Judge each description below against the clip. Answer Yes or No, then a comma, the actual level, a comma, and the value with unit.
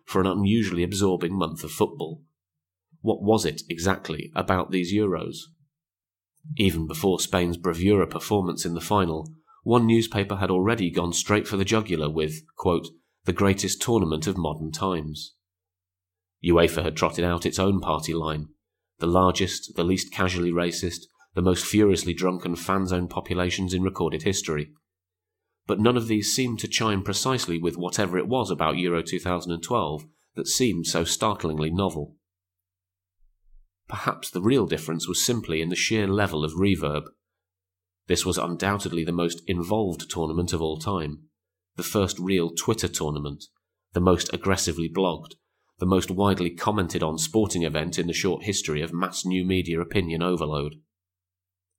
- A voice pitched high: No, very low, 90 Hz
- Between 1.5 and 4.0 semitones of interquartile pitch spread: Yes, narrow, 2.5 semitones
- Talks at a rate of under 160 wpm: Yes, average, 150 wpm